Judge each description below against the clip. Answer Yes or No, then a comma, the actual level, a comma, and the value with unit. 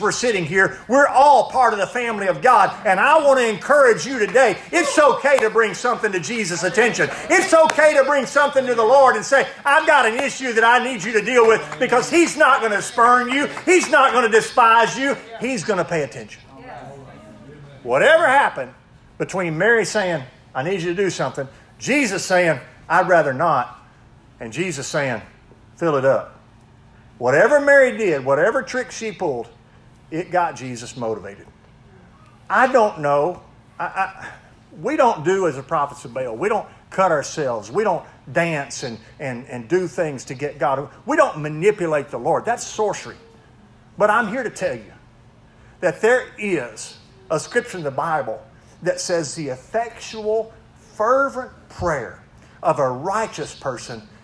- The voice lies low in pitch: No, medium, 185 Hz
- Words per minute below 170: No, average, 175 wpm